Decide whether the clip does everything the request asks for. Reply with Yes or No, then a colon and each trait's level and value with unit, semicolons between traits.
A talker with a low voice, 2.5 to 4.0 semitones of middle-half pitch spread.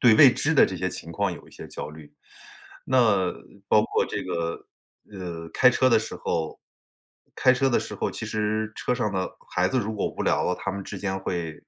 No: low, 100 Hz; average, 4.7 semitones